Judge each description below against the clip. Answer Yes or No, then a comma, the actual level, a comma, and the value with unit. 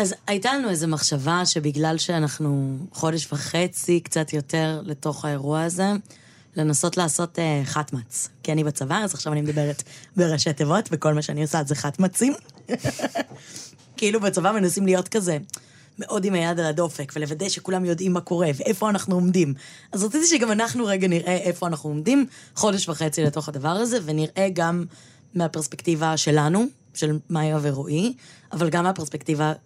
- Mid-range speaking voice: Yes, medium, 165 Hz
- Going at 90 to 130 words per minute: No, fast, 150 wpm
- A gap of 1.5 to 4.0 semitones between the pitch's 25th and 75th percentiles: Yes, average, 3.6 semitones